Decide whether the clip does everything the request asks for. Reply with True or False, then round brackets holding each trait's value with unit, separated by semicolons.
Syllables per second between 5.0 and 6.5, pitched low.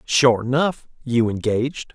False (4.1 syllables/s; 125 Hz)